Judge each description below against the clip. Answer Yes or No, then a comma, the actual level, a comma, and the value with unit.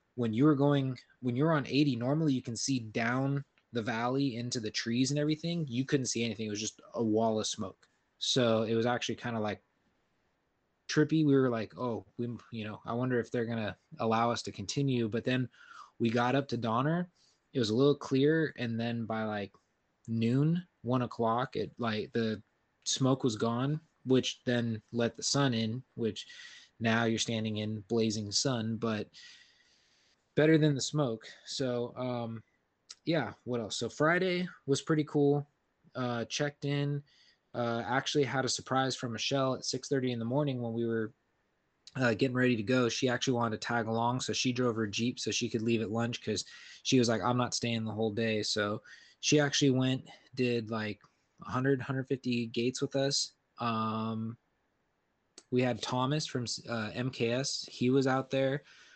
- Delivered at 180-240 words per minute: Yes, average, 185 wpm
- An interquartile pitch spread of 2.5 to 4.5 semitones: Yes, average, 3.2 semitones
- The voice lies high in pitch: No, low, 120 Hz